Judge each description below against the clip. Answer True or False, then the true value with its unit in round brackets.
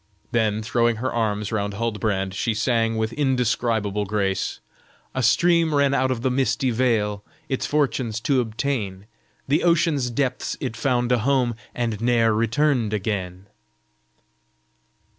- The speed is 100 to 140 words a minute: True (135 wpm)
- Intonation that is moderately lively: True (3.5 semitones)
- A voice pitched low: True (115 Hz)